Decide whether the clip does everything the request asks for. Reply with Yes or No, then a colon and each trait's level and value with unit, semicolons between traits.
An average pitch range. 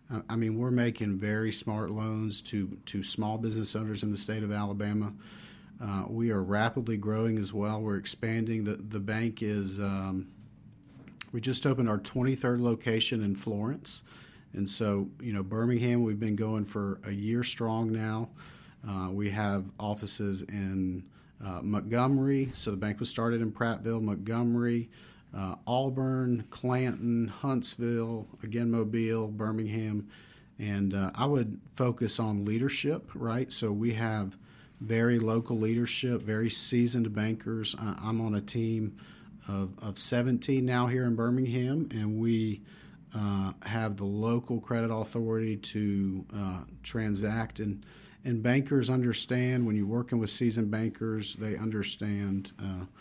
No: narrow, 2.3 semitones